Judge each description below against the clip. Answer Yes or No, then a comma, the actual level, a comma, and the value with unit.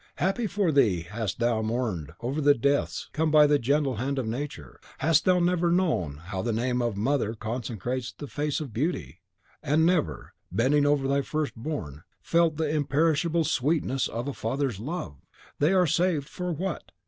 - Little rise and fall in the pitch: No, wide, 5.4 semitones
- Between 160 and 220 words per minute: Yes, average, 180 wpm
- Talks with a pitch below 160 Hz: Yes, medium, 140 Hz